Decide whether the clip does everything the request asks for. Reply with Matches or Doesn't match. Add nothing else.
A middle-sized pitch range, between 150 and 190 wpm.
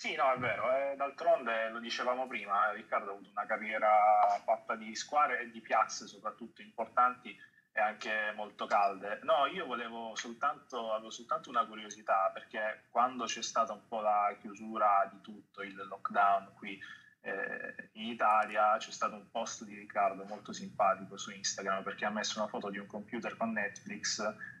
Matches